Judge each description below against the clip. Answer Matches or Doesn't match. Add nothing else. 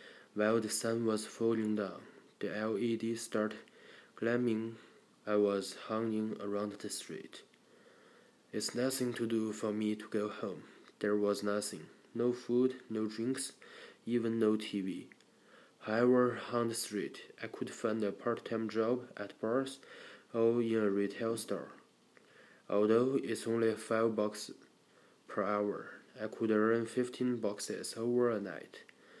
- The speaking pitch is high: Doesn't match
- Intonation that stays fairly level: Matches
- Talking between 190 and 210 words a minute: Doesn't match